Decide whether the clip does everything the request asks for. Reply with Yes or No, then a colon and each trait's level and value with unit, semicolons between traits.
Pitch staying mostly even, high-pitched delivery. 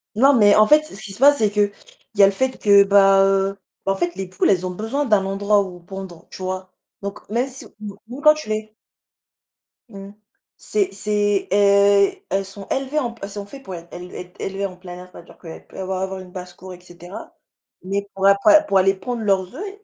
Yes: narrow, 2.2 semitones; high, 200 Hz